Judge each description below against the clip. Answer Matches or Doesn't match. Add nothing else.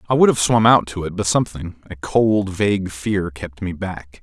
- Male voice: Matches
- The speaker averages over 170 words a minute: Matches